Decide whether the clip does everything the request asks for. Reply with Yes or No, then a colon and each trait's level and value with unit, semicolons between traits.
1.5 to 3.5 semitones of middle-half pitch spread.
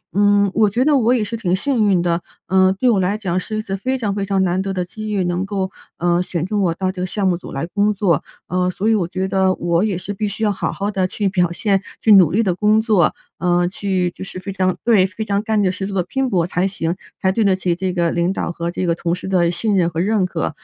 Yes: narrow, 2.5 semitones